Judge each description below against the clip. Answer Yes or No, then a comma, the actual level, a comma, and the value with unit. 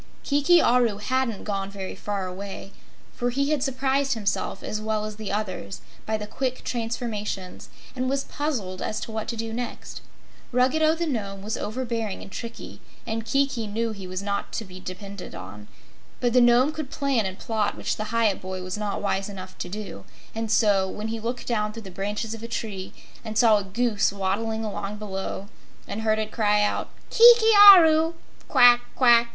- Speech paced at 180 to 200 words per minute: Yes, average, 190 wpm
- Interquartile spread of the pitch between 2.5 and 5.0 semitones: Yes, average, 3.6 semitones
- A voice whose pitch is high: Yes, high, 220 Hz